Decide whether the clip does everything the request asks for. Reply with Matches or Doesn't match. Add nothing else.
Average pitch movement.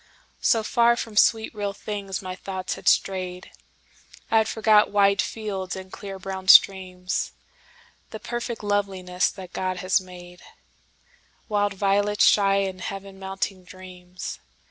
Doesn't match